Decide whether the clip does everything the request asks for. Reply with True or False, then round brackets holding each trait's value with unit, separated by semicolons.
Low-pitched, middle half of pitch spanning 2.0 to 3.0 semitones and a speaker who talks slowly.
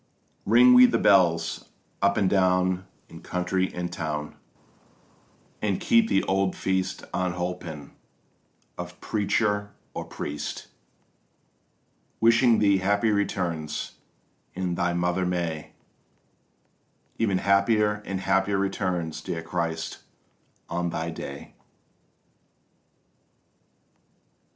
True (95 Hz; 2.7 semitones; 95 wpm)